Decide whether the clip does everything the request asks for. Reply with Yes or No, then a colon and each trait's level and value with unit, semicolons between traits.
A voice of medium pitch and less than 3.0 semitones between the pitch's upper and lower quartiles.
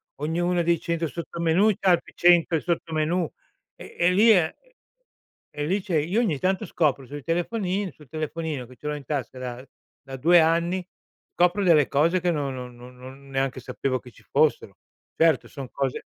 No: medium, 160 Hz; average, 4.3 semitones